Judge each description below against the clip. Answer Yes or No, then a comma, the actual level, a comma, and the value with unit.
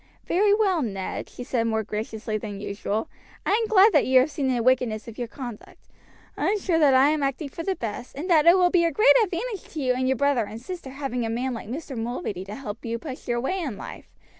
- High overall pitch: Yes, very high, 260 Hz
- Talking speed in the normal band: No, fast, 250 wpm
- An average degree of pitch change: No, wide, 6.4 semitones